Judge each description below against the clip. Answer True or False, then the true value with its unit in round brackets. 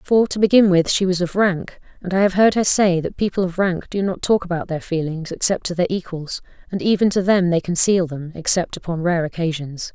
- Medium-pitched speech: True (180 Hz)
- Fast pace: True (235 wpm)